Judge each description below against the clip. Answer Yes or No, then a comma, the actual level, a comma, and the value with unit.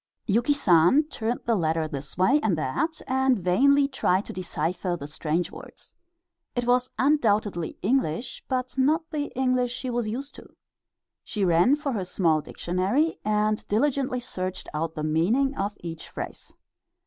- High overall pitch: Yes, high, 215 Hz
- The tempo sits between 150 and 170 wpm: Yes, average, 155 wpm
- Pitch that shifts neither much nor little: No, wide, 7.2 semitones